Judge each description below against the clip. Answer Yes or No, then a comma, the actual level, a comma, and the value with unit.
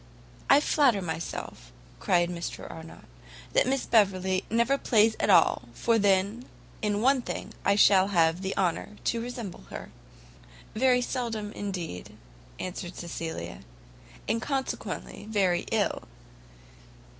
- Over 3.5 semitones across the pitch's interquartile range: Yes, average, 4.7 semitones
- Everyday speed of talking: No, slow, 120 wpm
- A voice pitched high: Yes, high, 200 Hz